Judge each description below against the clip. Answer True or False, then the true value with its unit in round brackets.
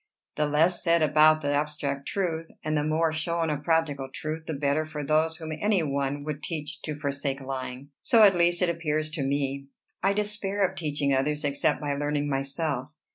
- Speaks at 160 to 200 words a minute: True (190 wpm)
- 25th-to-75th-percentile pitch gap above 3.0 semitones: False (2.4 semitones)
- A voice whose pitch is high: False (150 Hz)